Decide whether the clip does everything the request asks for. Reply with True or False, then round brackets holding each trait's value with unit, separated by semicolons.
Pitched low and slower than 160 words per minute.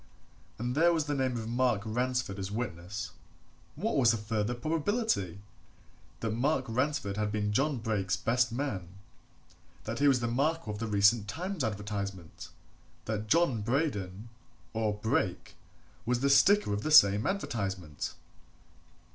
True (115 Hz; 145 wpm)